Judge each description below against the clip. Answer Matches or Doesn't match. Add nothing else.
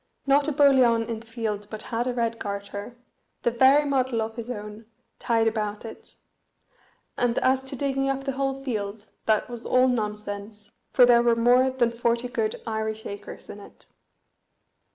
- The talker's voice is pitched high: Matches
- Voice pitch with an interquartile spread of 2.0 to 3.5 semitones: Matches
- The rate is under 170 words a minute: Doesn't match